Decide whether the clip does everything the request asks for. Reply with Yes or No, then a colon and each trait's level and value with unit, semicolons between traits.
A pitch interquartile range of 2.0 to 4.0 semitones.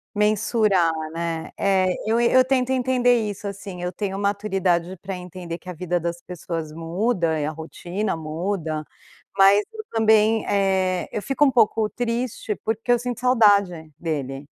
No: average, 4.5 semitones